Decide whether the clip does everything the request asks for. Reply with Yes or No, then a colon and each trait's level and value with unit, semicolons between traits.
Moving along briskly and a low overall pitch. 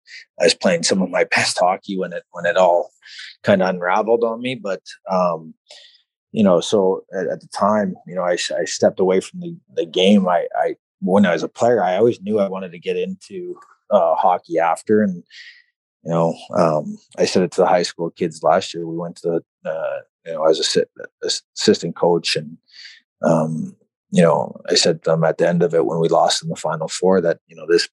Yes: fast, 230 wpm; low, 120 Hz